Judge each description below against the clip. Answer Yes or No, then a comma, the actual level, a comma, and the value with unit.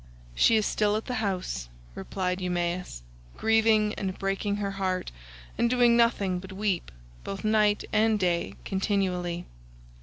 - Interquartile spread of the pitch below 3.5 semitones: Yes, average, 2.9 semitones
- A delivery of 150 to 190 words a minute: No, average, 140 wpm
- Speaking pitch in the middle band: No, high, 195 Hz